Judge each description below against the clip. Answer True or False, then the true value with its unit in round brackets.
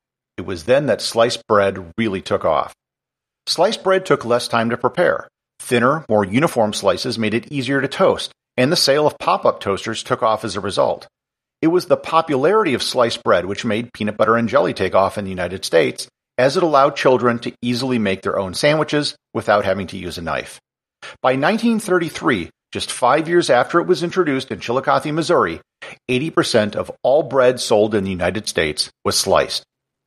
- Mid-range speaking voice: False (125 Hz)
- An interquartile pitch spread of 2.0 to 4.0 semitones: False (5.5 semitones)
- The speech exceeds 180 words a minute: True (190 wpm)